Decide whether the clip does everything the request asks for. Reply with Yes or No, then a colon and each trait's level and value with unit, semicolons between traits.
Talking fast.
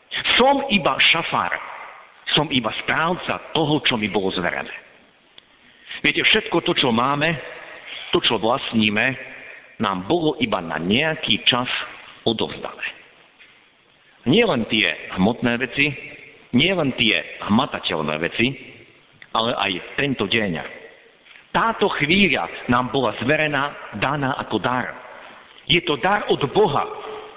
No: average, 115 wpm